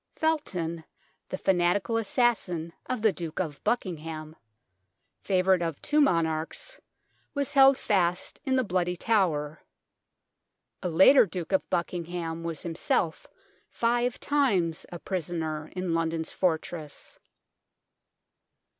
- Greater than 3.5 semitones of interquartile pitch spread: Yes, average, 5.1 semitones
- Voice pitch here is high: No, medium, 175 Hz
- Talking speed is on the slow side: Yes, slow, 110 wpm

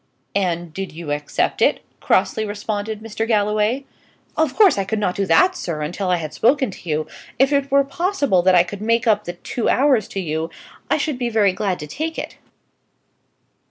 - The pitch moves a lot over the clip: Yes, wide, 6.0 semitones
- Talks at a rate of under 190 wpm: No, average, 195 wpm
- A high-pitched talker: Yes, high, 210 Hz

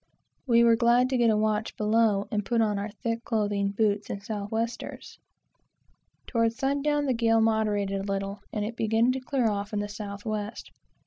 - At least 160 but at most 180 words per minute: No, average, 195 wpm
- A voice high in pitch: Yes, high, 220 Hz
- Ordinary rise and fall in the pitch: No, narrow, 2.1 semitones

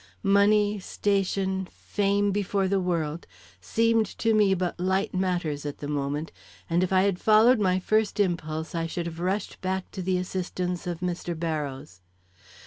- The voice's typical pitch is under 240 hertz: Yes, medium, 185 Hz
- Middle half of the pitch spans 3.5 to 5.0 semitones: No, average, 3.0 semitones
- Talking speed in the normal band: Yes, average, 160 wpm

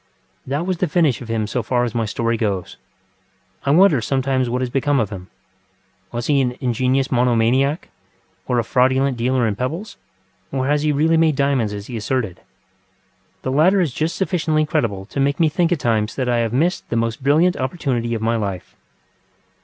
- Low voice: Yes, low, 130 Hz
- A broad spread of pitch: No, average, 4.2 semitones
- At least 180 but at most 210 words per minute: Yes, average, 195 wpm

